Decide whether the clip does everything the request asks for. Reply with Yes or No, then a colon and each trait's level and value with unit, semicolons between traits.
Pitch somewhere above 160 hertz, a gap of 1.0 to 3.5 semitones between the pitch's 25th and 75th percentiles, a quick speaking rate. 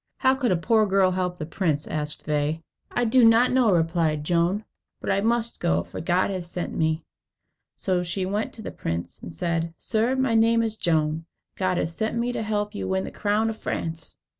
No: medium, 185 Hz; average, 5.2 semitones; fast, 215 wpm